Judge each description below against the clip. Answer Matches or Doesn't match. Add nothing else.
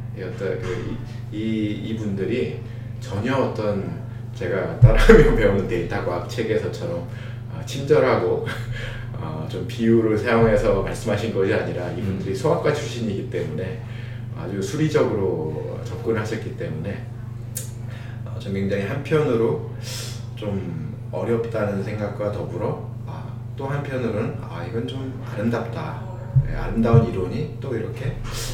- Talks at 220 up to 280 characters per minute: Matches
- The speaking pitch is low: Matches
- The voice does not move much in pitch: Matches